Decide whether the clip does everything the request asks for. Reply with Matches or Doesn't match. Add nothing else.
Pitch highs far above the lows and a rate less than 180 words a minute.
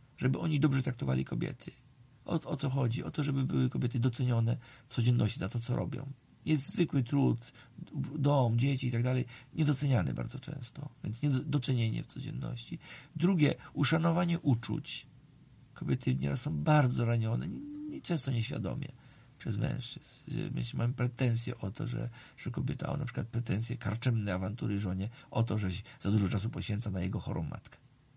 Doesn't match